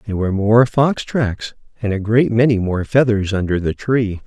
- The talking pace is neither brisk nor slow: Yes, average, 195 wpm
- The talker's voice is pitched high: No, low, 110 Hz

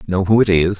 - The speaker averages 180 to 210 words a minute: No, fast, 300 wpm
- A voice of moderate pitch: No, very low, 95 Hz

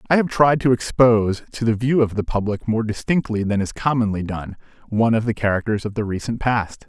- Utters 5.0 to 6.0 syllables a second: Yes, 5.7 syllables/s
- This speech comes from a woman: No, male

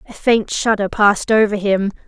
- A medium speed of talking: Yes, average, 175 wpm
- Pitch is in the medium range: No, high, 210 Hz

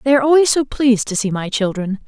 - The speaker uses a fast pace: Yes, fast, 260 wpm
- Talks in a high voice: Yes, high, 240 Hz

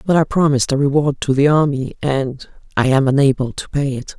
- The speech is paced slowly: No, average, 200 wpm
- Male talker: No, female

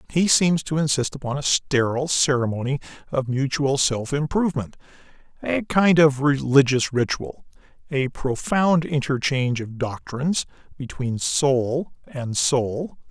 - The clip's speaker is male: Yes, male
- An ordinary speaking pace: No, slow, 120 wpm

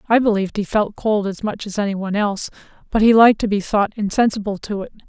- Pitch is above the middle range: Yes, high, 205 Hz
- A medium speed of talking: No, fast, 235 wpm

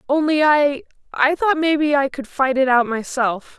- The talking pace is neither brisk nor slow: Yes, average, 165 wpm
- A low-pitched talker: No, very high, 280 Hz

